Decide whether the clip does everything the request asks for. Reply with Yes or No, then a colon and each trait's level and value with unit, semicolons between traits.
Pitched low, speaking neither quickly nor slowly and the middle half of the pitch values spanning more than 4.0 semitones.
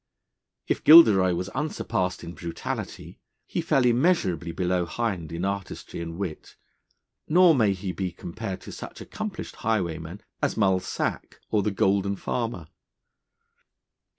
No: very low, 95 Hz; slow, 130 wpm; average, 4.4 semitones